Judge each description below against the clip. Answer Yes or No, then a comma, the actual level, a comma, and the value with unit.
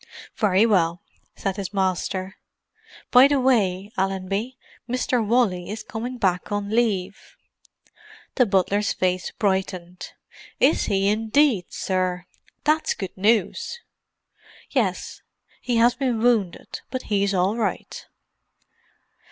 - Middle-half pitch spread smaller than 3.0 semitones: No, average, 3.9 semitones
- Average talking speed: No, slow, 110 wpm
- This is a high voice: Yes, high, 205 Hz